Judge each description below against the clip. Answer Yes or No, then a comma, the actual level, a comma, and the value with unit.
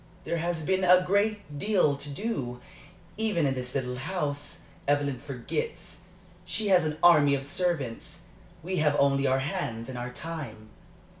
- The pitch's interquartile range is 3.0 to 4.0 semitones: No, average, 5.3 semitones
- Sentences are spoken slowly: No, average, 155 wpm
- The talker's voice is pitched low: No, medium, 145 Hz